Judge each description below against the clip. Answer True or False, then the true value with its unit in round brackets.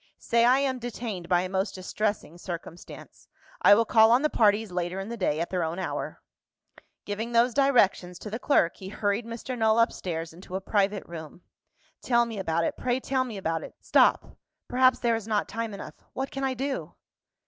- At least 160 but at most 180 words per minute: False (200 wpm)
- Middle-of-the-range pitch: False (215 Hz)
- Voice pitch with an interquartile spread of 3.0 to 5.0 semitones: True (4.6 semitones)